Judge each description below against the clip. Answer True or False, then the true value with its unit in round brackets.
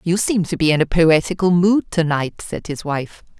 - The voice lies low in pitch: False (170 Hz)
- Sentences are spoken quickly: True (230 wpm)